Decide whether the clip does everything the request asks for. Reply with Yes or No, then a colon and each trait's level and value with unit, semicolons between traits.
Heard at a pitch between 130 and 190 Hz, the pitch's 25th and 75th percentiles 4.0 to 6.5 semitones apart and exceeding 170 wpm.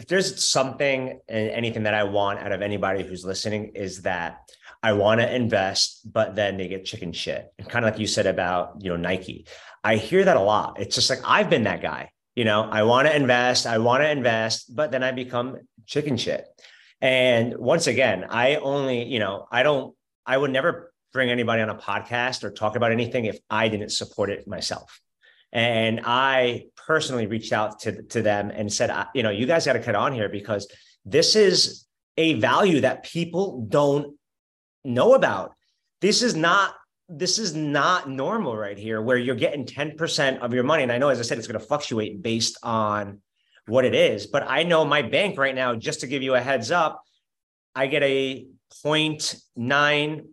No: low, 120 Hz; wide, 5.4 semitones; fast, 205 wpm